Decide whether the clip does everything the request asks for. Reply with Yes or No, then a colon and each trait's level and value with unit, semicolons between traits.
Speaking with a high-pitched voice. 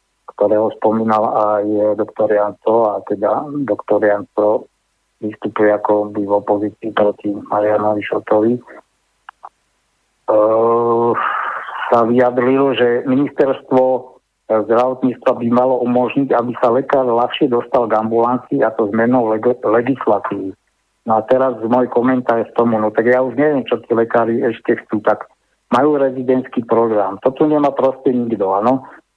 No: low, 115 Hz